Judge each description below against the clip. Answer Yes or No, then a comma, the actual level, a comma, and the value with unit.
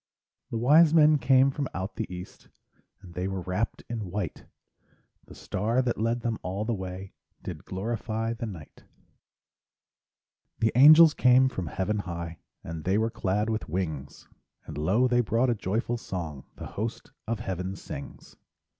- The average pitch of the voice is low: Yes, low, 105 Hz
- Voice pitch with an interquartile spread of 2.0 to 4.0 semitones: No, average, 4.5 semitones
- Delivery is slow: No, average, 160 wpm